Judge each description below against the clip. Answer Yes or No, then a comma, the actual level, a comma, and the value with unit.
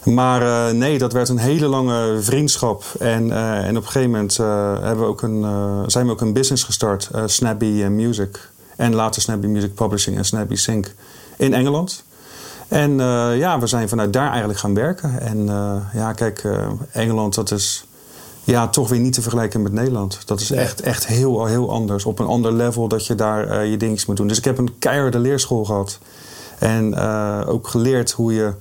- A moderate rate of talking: No, fast, 205 wpm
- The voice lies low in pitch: Yes, low, 115 Hz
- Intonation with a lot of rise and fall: No, average, 2.9 semitones